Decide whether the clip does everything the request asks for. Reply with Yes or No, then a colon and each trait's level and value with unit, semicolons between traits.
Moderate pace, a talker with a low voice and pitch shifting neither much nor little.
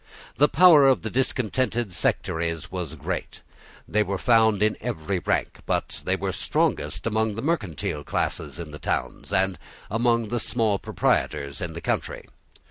No: average, 155 wpm; low, 105 Hz; wide, 5.9 semitones